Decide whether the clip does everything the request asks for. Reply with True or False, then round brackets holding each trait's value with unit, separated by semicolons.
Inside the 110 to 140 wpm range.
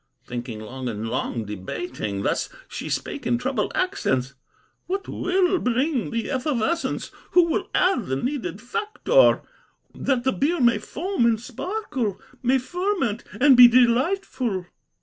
True (135 wpm)